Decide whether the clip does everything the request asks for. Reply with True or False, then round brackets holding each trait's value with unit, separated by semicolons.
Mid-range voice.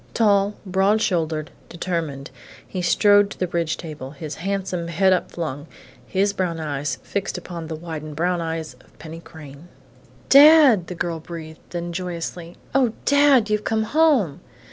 True (175 Hz)